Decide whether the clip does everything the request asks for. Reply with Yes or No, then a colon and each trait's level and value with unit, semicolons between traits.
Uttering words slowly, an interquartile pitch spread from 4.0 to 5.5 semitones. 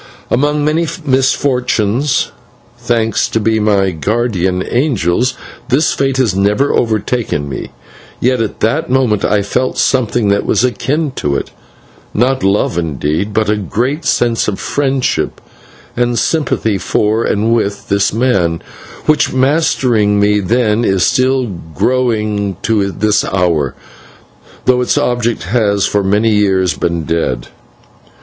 Yes: slow, 130 wpm; average, 4.3 semitones